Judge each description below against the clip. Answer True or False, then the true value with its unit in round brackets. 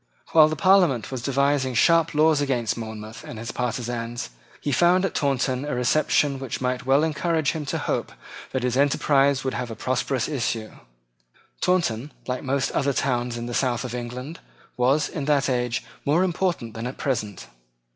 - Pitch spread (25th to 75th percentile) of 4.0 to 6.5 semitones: False (3.4 semitones)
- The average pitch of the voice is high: False (130 Hz)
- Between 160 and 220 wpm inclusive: True (175 wpm)